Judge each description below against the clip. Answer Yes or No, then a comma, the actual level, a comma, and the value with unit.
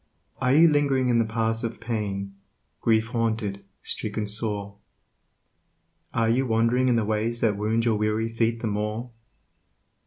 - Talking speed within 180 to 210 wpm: No, average, 150 wpm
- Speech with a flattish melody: Yes, narrow, 1.7 semitones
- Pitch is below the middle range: Yes, low, 115 Hz